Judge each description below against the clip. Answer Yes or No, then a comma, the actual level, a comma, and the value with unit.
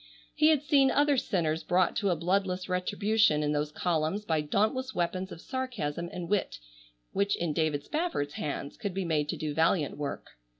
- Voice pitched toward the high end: No, medium, 180 Hz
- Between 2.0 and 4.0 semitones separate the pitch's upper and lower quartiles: No, average, 5.2 semitones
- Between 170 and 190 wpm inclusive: Yes, average, 180 wpm